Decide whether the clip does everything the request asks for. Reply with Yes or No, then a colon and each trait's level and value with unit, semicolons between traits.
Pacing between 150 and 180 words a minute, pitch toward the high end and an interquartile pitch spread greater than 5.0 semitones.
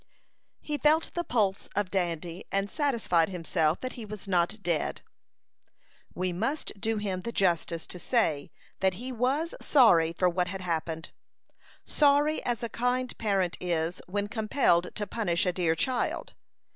Yes: average, 155 wpm; high, 195 Hz; wide, 5.6 semitones